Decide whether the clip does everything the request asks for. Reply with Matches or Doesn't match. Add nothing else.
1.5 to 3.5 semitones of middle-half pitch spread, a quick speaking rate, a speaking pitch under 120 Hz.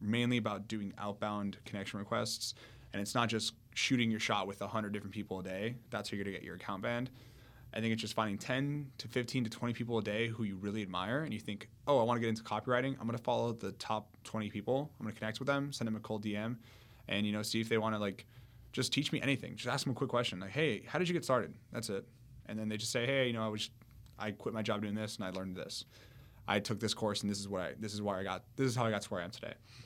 Matches